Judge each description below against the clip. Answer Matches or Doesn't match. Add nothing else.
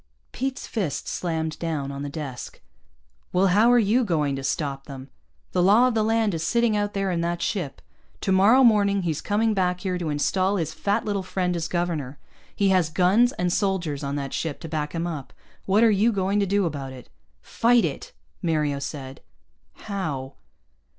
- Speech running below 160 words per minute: Doesn't match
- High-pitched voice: Doesn't match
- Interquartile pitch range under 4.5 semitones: Doesn't match